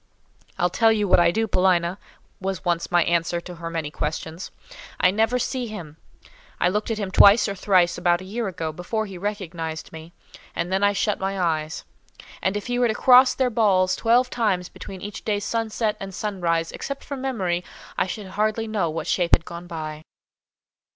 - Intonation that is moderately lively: Yes, average, 4.0 semitones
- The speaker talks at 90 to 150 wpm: No, average, 195 wpm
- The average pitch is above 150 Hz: Yes, high, 190 Hz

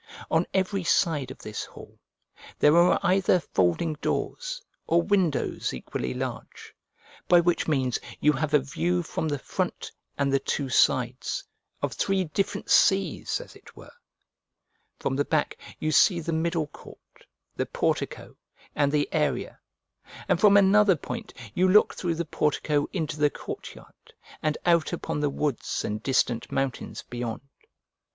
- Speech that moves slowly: No, average, 150 wpm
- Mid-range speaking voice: Yes, medium, 155 Hz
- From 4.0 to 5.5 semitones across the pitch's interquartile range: Yes, average, 4.3 semitones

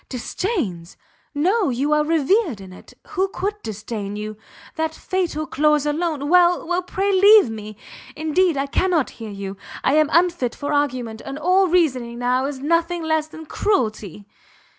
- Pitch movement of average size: No, wide, 6.4 semitones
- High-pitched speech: Yes, very high, 300 Hz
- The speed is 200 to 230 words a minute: No, average, 160 wpm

